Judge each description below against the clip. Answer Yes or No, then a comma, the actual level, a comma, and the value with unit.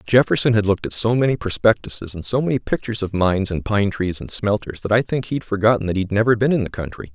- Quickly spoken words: Yes, fast, 250 wpm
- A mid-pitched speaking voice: No, low, 105 Hz